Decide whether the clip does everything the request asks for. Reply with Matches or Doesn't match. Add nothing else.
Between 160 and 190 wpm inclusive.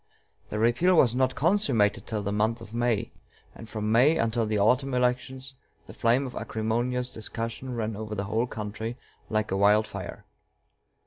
Matches